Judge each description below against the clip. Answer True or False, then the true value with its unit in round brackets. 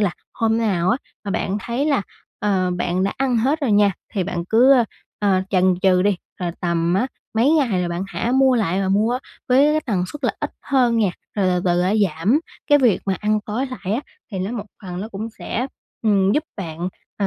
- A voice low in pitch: False (205 Hz)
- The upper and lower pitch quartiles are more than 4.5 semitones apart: True (4.9 semitones)